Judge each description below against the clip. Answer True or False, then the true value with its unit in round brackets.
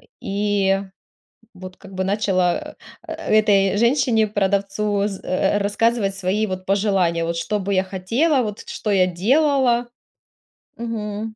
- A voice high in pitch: True (205 Hz)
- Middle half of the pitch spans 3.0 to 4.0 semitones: False (2.5 semitones)